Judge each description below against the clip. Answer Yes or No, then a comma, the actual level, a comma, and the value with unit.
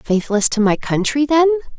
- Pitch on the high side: Yes, very high, 255 Hz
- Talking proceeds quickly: No, average, 170 wpm